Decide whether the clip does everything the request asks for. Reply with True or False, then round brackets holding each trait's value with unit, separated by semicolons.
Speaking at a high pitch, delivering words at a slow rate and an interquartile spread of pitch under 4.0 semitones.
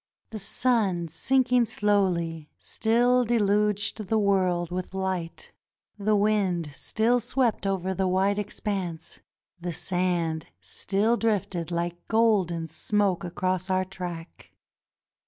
True (195 Hz; 110 wpm; 3.4 semitones)